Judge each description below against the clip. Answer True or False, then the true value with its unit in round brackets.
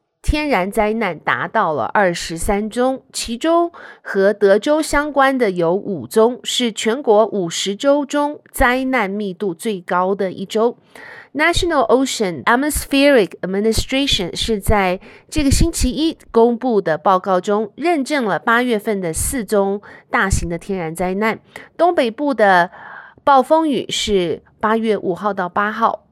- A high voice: True (220 Hz)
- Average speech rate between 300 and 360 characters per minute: False (275 characters per minute)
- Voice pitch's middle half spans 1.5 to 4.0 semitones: False (5.4 semitones)